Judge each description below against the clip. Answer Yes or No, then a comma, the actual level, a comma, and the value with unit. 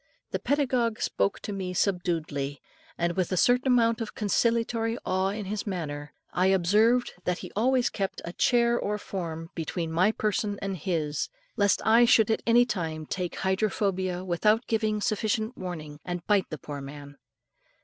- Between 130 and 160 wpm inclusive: No, average, 170 wpm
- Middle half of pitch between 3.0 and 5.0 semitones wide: Yes, average, 4.6 semitones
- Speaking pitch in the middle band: No, high, 195 Hz